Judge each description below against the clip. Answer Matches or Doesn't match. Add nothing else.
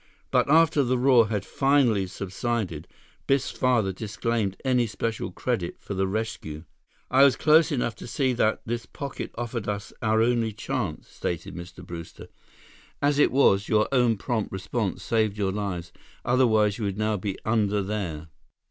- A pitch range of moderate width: Matches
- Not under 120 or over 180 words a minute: Matches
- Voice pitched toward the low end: Matches